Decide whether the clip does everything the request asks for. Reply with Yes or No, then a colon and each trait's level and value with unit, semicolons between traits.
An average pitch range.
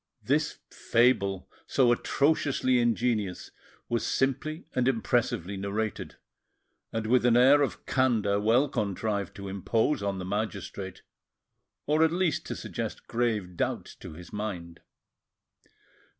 Yes: average, 4.4 semitones